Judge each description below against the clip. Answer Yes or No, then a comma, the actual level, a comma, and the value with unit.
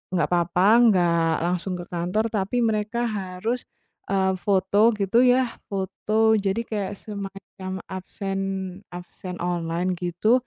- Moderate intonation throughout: Yes, average, 3.1 semitones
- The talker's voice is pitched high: Yes, high, 195 Hz